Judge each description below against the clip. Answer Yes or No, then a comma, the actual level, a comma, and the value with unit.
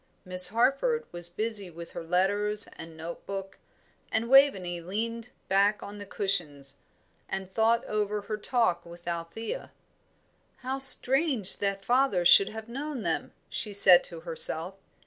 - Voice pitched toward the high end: Yes, high, 200 Hz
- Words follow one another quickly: No, average, 145 wpm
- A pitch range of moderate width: Yes, average, 4.7 semitones